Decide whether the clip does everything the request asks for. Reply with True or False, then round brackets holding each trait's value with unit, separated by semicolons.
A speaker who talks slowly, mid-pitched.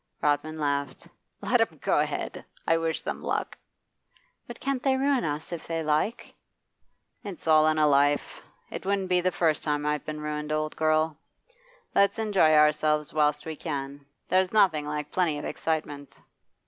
False (165 wpm; 155 Hz)